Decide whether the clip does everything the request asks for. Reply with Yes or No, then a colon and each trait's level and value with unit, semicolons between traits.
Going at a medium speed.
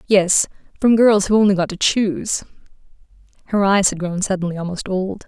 Yes: average, 170 wpm